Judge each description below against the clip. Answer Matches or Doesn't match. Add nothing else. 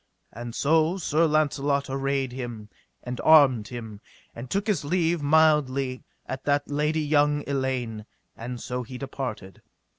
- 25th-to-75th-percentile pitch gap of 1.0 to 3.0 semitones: Doesn't match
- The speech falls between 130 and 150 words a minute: Matches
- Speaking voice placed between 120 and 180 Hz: Matches